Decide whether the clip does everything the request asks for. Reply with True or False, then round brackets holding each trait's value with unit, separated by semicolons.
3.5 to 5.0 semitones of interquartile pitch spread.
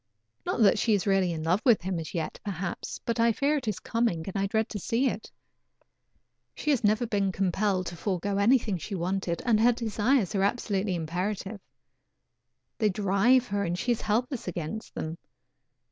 True (3.8 semitones)